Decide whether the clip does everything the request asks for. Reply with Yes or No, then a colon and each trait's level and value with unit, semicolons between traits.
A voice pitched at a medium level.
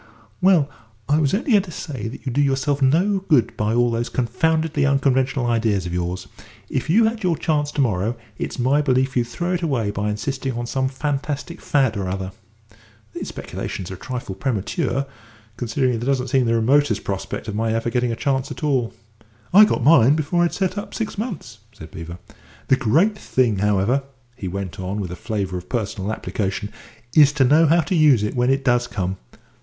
No: low, 130 Hz